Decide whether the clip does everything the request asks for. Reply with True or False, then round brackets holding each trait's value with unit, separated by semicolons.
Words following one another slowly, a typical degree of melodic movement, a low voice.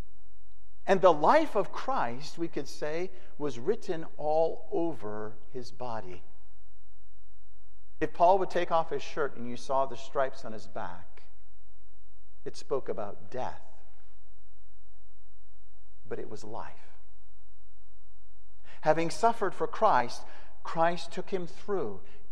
False (120 wpm; 7.2 semitones; 120 Hz)